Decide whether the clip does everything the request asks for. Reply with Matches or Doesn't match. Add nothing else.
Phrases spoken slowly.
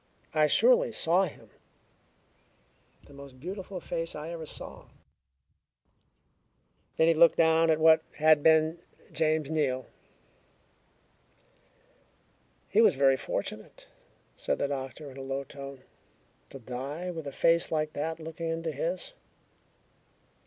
Matches